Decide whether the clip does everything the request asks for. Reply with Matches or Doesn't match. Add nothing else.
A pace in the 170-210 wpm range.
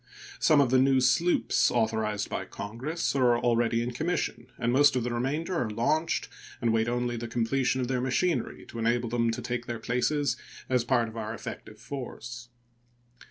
Matches